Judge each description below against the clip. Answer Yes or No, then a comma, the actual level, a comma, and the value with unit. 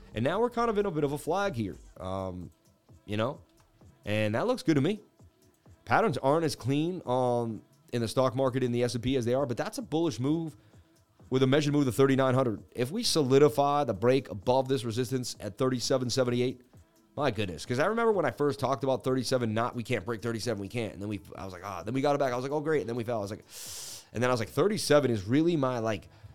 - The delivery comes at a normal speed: No, fast, 255 wpm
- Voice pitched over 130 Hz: No, low, 125 Hz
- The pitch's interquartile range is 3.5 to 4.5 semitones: Yes, average, 4.2 semitones